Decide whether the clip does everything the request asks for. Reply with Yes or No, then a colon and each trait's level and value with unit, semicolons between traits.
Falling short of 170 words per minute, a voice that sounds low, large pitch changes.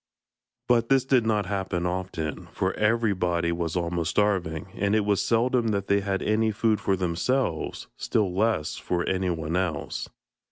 No: average, 155 wpm; very low, 95 Hz; average, 3.9 semitones